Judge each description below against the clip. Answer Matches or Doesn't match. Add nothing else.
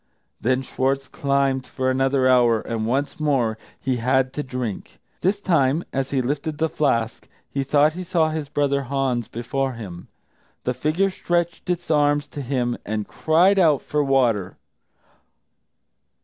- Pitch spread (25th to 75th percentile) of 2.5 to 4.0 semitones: Matches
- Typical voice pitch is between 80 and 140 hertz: Matches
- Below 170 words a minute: Matches